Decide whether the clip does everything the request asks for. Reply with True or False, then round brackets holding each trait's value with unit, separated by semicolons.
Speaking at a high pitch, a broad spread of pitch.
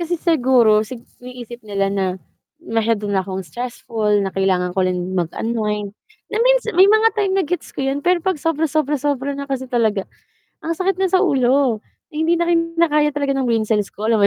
True (255 Hz; 7.7 semitones)